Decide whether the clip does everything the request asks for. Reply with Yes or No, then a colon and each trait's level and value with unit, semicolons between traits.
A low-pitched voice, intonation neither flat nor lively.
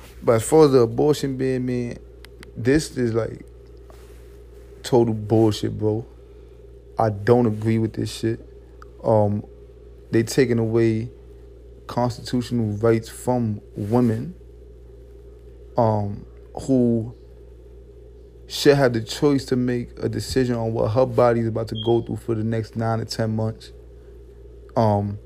No: low, 115 Hz; narrow, 1.9 semitones